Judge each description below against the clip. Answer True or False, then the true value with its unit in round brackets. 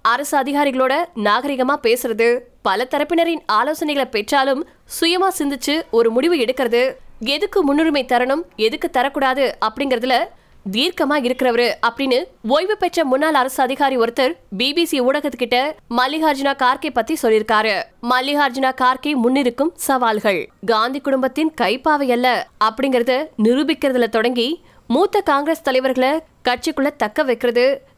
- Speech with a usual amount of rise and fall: True (3.8 semitones)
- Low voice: False (270 Hz)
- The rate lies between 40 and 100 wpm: False (110 wpm)